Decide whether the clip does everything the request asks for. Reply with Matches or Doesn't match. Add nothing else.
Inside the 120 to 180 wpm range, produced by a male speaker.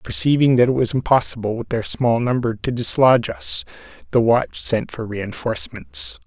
Matches